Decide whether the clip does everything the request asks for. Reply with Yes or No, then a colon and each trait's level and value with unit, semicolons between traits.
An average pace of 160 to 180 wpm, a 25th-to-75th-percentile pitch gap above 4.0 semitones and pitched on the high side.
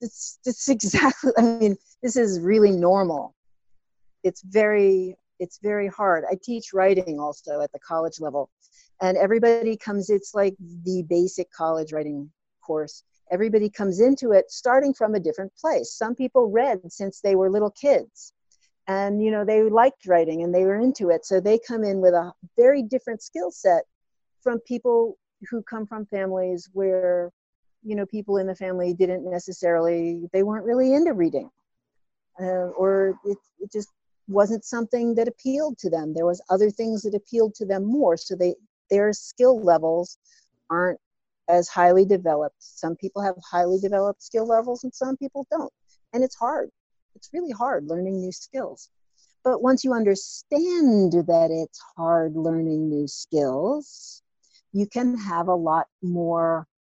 Yes: average, 165 wpm; average, 4.7 semitones; high, 200 Hz